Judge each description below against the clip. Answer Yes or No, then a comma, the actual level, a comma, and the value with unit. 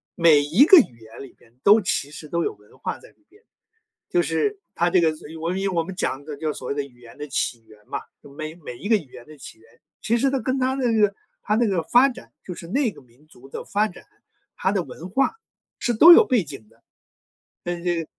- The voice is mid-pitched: Yes, medium, 170 Hz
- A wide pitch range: Yes, wide, 7.8 semitones